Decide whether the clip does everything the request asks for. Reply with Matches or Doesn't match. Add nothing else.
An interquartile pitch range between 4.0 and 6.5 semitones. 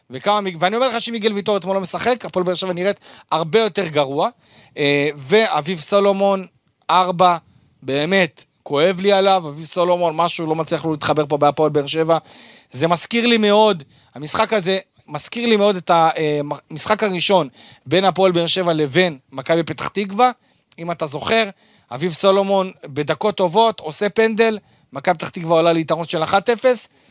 Matches